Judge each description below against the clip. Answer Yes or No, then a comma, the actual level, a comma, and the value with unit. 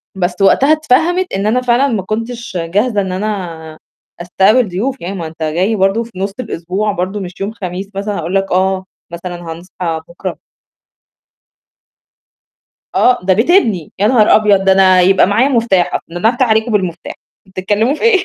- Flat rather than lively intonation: No, average, 4.0 semitones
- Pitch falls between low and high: No, high, 195 Hz